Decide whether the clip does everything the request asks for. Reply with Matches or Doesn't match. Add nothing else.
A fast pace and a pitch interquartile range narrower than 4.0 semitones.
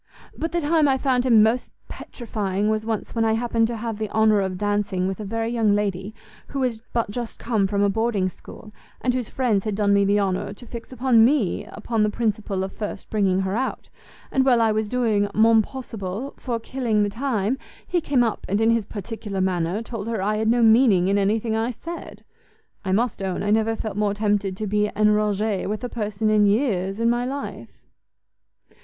Matches